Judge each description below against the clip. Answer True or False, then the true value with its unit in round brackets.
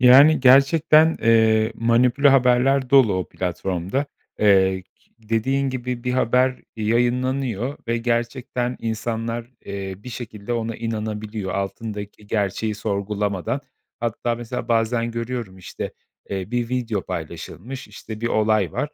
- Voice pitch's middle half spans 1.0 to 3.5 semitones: True (3.1 semitones)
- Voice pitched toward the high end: False (115 Hz)